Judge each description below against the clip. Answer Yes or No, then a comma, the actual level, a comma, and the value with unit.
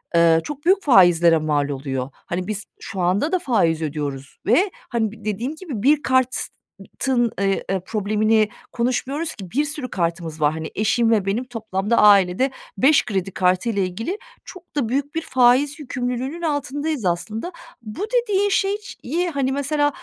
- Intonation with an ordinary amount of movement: No, wide, 7.5 semitones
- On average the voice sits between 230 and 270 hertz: Yes, high, 235 Hz